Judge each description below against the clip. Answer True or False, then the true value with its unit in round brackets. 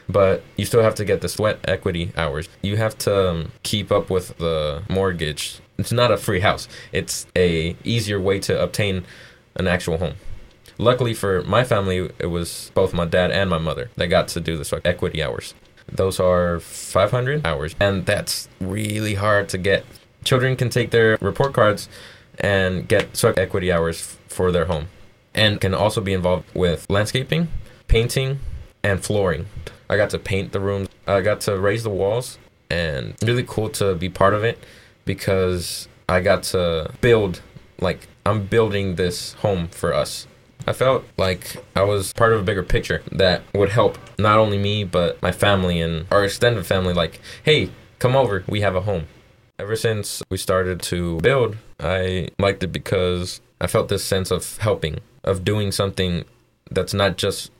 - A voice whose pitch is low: True (100 Hz)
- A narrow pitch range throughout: False (3.2 semitones)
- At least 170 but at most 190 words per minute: True (180 wpm)